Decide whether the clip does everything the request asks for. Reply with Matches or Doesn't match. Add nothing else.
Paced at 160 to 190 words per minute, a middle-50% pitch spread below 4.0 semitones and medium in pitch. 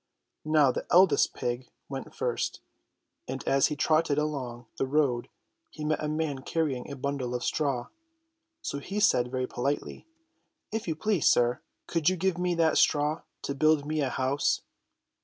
Matches